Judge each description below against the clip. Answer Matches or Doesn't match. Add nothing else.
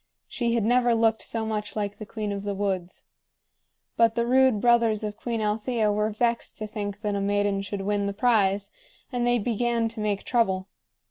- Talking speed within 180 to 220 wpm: Matches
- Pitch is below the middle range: Doesn't match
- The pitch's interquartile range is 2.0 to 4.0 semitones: Matches